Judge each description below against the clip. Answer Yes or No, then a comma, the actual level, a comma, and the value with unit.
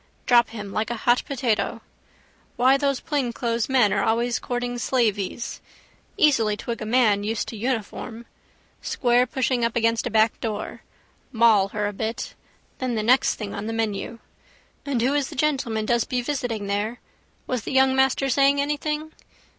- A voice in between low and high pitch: No, high, 235 Hz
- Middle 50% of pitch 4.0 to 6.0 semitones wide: No, average, 3.1 semitones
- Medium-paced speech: Yes, average, 160 wpm